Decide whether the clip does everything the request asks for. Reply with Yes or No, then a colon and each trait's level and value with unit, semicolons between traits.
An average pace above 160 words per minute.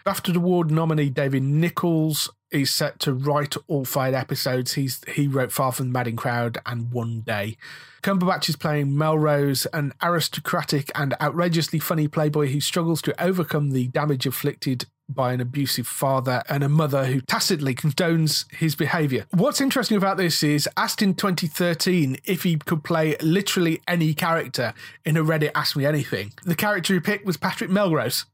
Yes: average, 170 wpm